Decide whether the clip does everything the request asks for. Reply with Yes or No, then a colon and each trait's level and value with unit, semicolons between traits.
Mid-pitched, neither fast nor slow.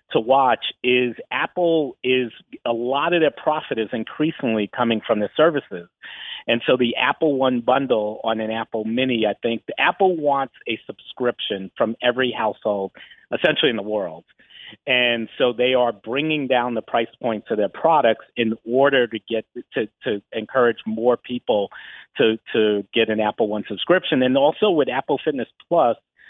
No: low, 120 Hz; average, 170 wpm